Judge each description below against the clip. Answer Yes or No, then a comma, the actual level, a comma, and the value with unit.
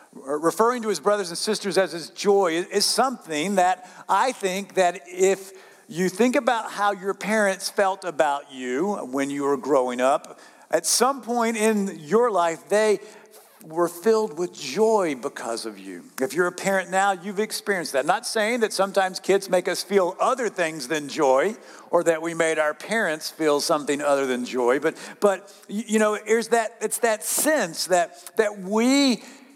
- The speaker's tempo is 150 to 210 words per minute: Yes, average, 180 wpm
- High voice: Yes, high, 195 Hz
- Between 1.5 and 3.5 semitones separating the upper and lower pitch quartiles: No, average, 4.4 semitones